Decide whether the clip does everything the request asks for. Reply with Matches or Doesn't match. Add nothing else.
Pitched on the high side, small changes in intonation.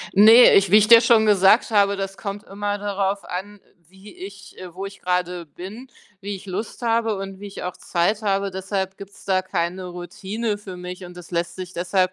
Matches